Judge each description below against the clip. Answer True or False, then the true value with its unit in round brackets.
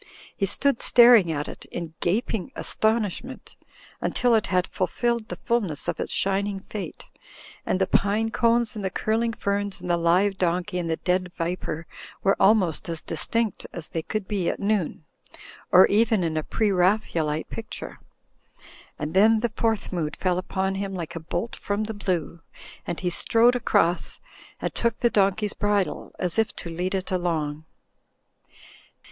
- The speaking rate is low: False (165 wpm)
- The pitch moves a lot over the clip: False (3.9 semitones)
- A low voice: False (195 Hz)